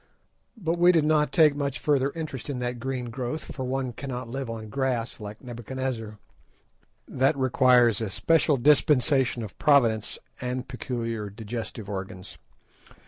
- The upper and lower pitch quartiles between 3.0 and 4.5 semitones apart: Yes, average, 3.3 semitones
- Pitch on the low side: Yes, low, 125 Hz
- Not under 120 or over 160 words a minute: Yes, average, 140 wpm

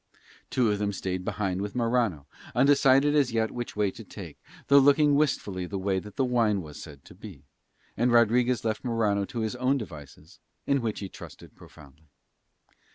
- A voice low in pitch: Yes, low, 110 Hz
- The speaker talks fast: No, average, 180 wpm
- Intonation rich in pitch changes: No, average, 4.7 semitones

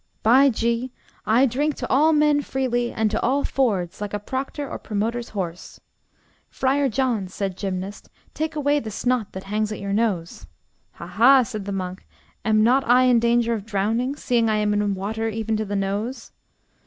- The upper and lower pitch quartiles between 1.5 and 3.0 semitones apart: No, average, 4.1 semitones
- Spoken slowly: No, average, 185 wpm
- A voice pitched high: Yes, high, 225 Hz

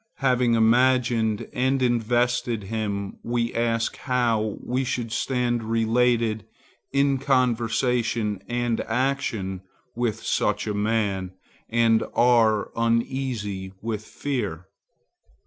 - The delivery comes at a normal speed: No, slow, 95 wpm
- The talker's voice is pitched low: Yes, low, 115 Hz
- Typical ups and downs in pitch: No, narrow, 2.2 semitones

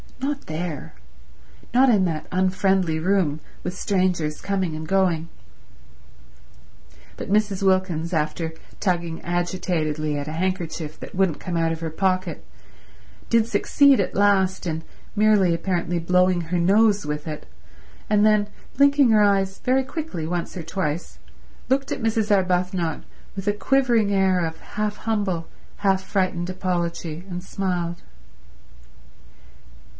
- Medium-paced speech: No, slow, 130 wpm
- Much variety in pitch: No, average, 3.3 semitones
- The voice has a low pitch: No, medium, 185 Hz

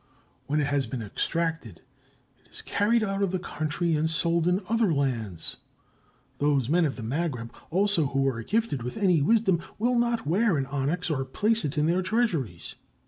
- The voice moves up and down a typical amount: No, wide, 6.3 semitones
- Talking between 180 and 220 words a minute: Yes, average, 185 wpm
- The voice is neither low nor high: Yes, medium, 160 Hz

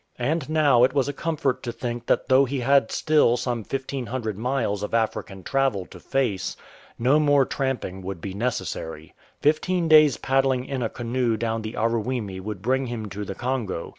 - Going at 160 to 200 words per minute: Yes, average, 180 wpm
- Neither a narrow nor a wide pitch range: Yes, average, 3.8 semitones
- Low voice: Yes, low, 125 Hz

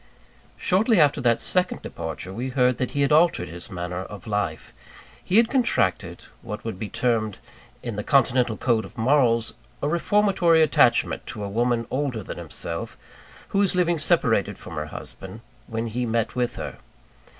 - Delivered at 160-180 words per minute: Yes, average, 170 wpm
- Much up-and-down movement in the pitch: Yes, wide, 6.2 semitones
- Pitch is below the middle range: Yes, low, 120 Hz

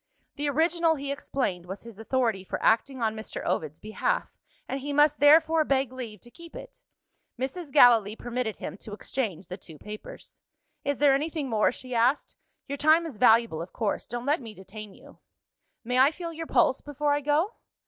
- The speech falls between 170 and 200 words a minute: Yes, average, 190 wpm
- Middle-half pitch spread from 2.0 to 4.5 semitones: No, average, 5.1 semitones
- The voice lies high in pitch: Yes, very high, 260 Hz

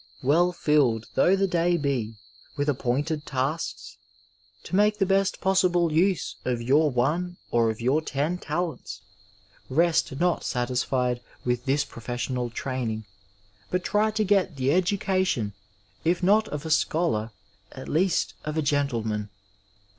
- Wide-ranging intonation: Yes, wide, 6.1 semitones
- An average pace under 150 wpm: Yes, average, 140 wpm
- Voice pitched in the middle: Yes, medium, 150 Hz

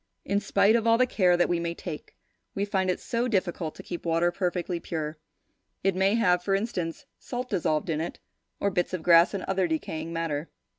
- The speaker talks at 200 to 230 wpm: Yes, fast, 205 wpm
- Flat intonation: No, average, 3.0 semitones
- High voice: No, medium, 180 Hz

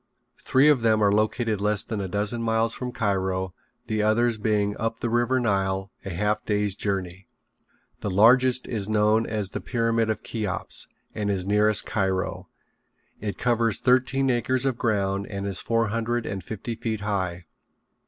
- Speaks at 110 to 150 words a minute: No, average, 165 wpm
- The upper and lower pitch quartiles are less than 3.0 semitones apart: Yes, narrow, 2.6 semitones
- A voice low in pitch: Yes, low, 110 Hz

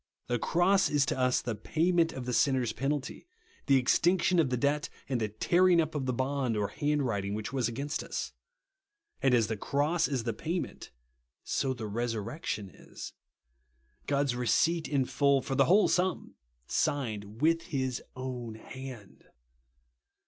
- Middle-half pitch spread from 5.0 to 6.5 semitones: No, average, 4.0 semitones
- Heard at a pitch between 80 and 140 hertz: Yes, low, 135 Hz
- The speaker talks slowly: No, average, 160 wpm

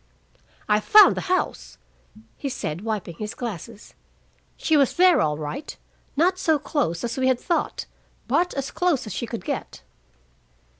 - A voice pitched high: Yes, very high, 255 Hz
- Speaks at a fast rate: No, average, 155 wpm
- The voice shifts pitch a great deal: Yes, wide, 7.6 semitones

